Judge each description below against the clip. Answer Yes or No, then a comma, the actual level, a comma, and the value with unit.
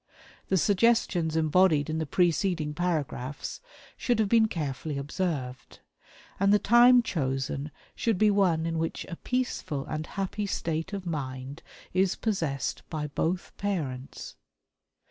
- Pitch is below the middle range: No, medium, 165 Hz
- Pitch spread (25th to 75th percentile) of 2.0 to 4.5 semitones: No, average, 5.0 semitones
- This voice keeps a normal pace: No, slow, 130 wpm